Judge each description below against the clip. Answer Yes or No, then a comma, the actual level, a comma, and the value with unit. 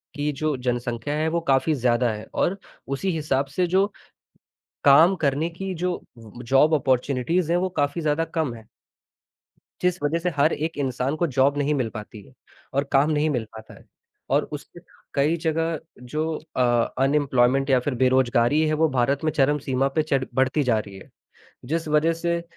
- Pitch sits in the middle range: Yes, medium, 145 Hz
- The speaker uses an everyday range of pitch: Yes, average, 3.7 semitones